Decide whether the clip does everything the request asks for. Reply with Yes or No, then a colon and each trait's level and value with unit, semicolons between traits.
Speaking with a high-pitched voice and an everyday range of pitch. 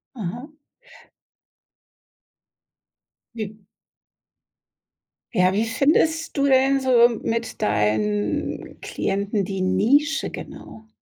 No: high, 225 Hz; wide, 6.4 semitones